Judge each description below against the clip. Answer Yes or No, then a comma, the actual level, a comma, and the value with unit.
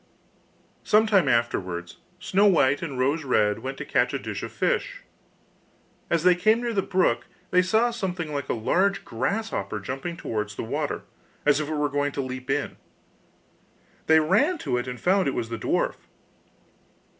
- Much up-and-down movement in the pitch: Yes, wide, 7.2 semitones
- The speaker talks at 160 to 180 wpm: Yes, average, 175 wpm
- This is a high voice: No, medium, 150 Hz